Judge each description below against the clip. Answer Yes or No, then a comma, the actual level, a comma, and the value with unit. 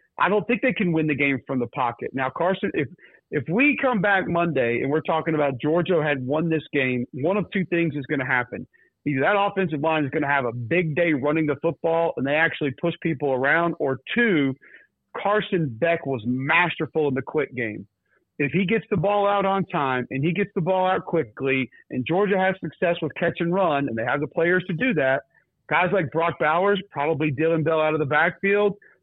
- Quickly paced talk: Yes, fast, 225 wpm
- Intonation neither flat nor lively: Yes, average, 4.4 semitones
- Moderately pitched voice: Yes, medium, 165 Hz